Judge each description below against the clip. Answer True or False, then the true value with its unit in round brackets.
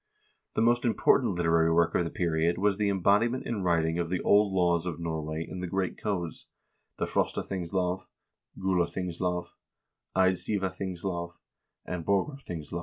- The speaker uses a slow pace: False (160 wpm)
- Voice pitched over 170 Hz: False (90 Hz)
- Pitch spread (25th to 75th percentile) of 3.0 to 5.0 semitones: False (2.4 semitones)